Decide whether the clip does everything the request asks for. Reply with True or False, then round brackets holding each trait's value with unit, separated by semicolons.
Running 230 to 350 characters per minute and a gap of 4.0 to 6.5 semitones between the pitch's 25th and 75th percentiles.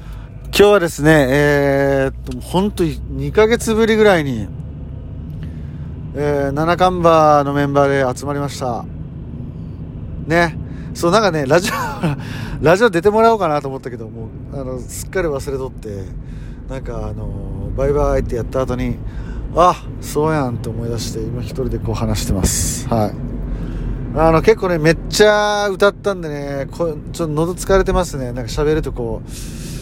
True (320 characters per minute; 5.1 semitones)